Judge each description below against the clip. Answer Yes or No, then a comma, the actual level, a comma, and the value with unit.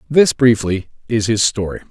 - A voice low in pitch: Yes, low, 115 Hz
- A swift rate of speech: No, average, 155 wpm